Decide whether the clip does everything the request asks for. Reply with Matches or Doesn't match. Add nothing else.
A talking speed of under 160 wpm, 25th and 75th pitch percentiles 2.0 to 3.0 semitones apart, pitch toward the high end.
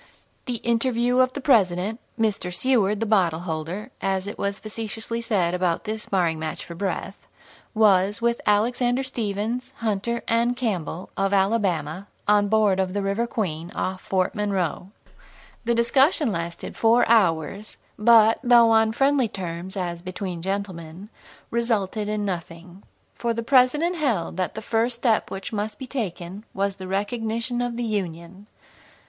Doesn't match